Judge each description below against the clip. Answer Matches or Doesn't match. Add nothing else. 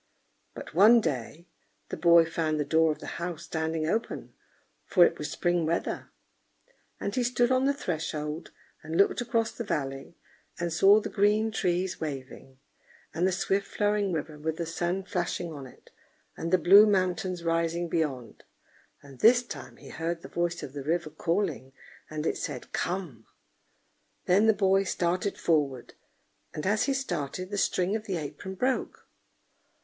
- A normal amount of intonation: Matches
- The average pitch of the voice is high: Doesn't match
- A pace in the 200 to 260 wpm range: Doesn't match